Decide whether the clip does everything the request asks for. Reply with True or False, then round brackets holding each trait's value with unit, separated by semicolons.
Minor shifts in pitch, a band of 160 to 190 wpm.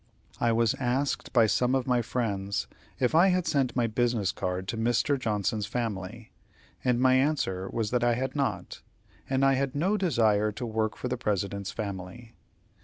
False (3.7 semitones; 180 wpm)